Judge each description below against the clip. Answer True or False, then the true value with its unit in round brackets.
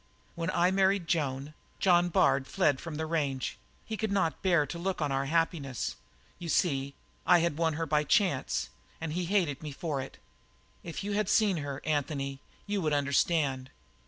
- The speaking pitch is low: False (160 Hz)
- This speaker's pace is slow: False (185 wpm)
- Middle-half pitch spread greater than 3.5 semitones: True (3.9 semitones)